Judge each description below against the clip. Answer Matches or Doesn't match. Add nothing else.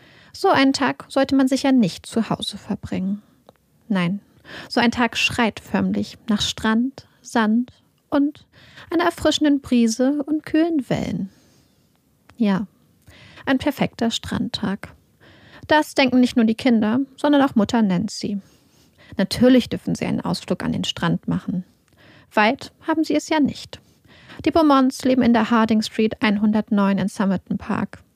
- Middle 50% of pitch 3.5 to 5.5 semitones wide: Matches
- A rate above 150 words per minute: Doesn't match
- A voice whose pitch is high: Matches